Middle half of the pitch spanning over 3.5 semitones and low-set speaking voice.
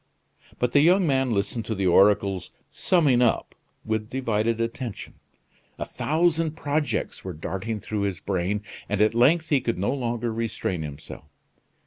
Yes: average, 5.1 semitones; low, 115 Hz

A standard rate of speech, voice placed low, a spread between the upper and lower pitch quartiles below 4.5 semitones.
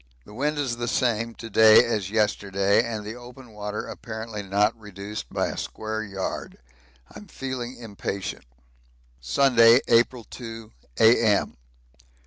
No: slow, 130 wpm; low, 110 Hz; narrow, 2.4 semitones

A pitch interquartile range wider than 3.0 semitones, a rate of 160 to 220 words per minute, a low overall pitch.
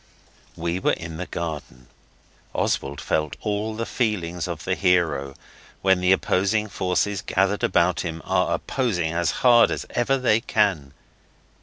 No: average, 4.2 semitones; average, 145 wpm; very low, 90 Hz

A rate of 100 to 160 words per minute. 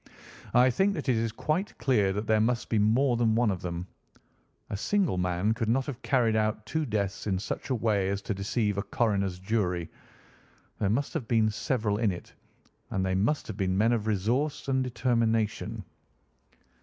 No: average, 190 wpm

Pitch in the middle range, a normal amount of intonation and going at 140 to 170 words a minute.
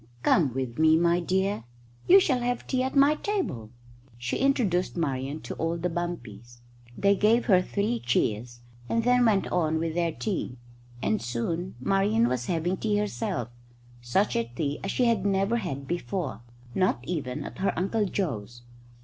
No: medium, 175 Hz; wide, 7.8 semitones; average, 165 wpm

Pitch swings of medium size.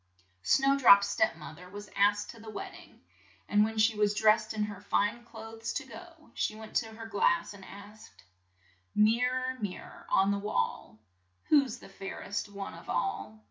No: narrow, 2.2 semitones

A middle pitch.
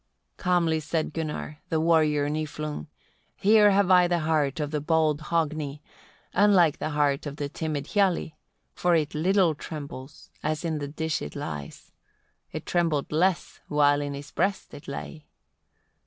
Yes: medium, 155 Hz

